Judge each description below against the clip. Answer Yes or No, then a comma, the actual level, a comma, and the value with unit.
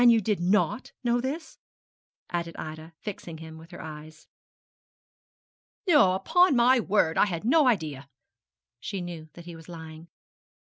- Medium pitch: Yes, medium, 175 Hz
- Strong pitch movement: Yes, wide, 6.6 semitones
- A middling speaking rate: Yes, average, 145 wpm